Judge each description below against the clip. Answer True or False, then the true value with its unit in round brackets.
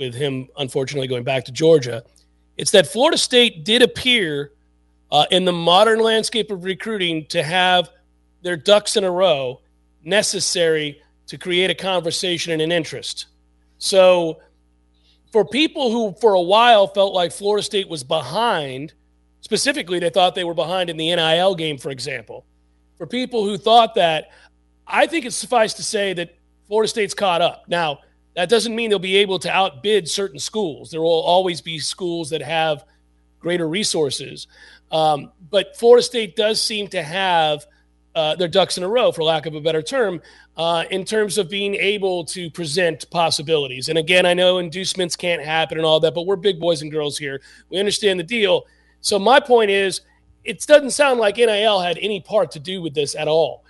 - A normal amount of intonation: True (4.7 semitones)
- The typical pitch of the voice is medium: True (175 Hz)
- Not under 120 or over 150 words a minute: False (185 wpm)